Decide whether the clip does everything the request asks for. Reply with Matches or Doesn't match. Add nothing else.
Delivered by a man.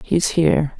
Doesn't match